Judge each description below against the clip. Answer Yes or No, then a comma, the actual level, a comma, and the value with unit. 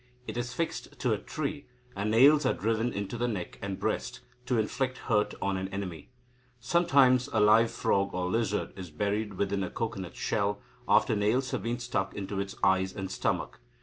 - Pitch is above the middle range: No, low, 105 Hz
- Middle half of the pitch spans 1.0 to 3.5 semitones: No, average, 3.9 semitones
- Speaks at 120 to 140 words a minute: No, average, 185 wpm